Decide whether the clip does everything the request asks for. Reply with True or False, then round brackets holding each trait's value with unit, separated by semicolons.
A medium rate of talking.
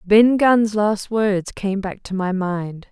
True (185 wpm)